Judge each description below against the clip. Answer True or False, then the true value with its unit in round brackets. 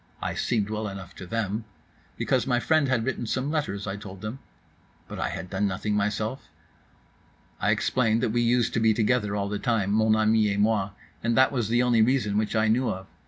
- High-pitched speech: False (110 Hz)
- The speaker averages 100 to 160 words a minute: False (195 wpm)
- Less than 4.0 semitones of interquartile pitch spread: True (2.9 semitones)